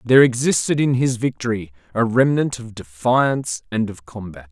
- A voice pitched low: Yes, low, 115 Hz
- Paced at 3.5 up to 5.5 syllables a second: Yes, 5.1 syllables/s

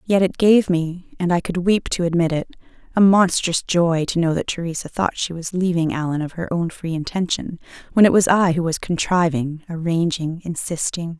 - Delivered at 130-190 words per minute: No, average, 200 wpm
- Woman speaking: Yes, female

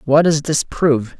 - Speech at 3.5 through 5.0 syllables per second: Yes, 4.7 syllables/s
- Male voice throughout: Yes, male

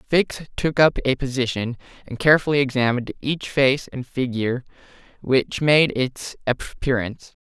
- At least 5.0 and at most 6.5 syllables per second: No, 4.8 syllables/s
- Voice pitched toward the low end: Yes, low, 130 Hz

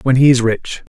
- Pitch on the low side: Yes, low, 125 Hz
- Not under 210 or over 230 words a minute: No, fast, 255 wpm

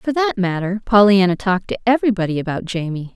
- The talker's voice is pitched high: Yes, high, 200 Hz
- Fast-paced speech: No, average, 170 wpm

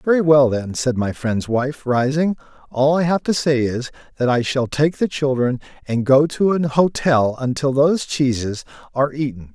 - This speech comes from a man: Yes, male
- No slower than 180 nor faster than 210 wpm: Yes, average, 190 wpm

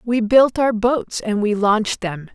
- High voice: Yes, high, 220 Hz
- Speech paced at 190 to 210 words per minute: Yes, fast, 205 wpm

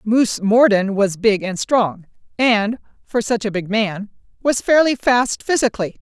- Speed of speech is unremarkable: Yes, average, 160 wpm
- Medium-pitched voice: No, high, 220 Hz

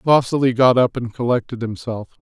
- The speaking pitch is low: Yes, low, 120 Hz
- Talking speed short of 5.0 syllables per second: No, 5.5 syllables/s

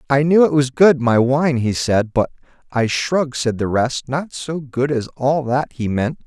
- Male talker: Yes, male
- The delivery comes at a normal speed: No, fast, 220 wpm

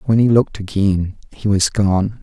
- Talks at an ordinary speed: Yes, average, 190 wpm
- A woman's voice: No, male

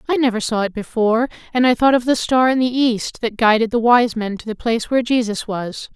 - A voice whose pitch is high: Yes, high, 230 Hz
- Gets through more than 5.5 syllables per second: Yes, 5.8 syllables/s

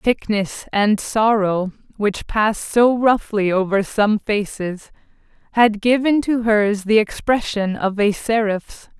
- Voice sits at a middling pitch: No, high, 210 Hz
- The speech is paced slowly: Yes, slow, 125 wpm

